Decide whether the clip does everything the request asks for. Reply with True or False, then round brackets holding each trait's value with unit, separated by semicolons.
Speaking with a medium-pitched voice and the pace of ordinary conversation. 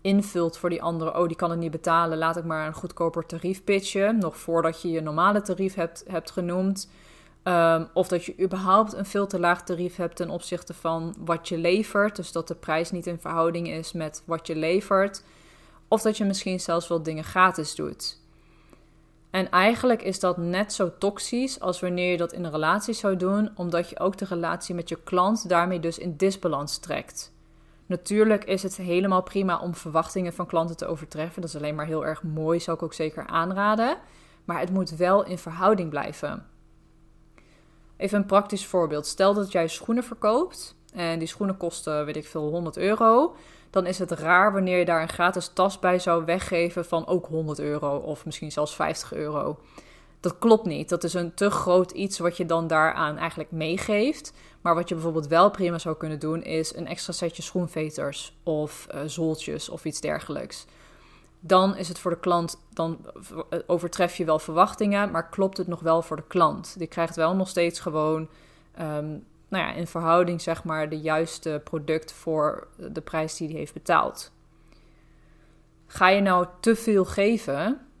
True (175 Hz; 190 wpm)